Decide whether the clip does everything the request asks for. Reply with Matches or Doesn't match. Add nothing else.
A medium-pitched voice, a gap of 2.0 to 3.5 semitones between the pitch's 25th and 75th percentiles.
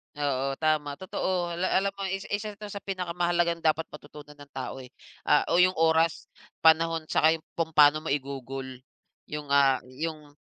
Matches